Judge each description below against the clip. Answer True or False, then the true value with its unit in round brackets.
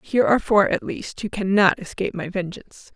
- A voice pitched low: False (195 Hz)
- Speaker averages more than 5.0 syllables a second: True (6.0 syllables/s)